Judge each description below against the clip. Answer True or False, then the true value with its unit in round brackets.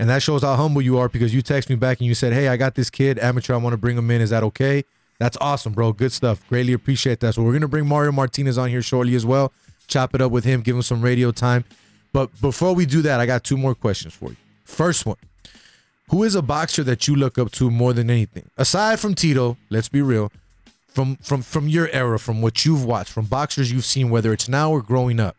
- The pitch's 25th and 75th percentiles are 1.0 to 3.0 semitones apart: True (2.7 semitones)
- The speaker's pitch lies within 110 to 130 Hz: True (125 Hz)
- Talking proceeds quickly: True (260 wpm)